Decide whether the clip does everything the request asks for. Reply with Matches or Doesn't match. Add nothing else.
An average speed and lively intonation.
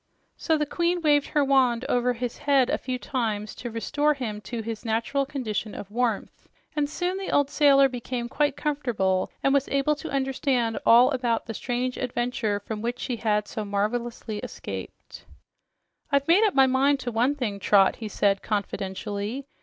Doesn't match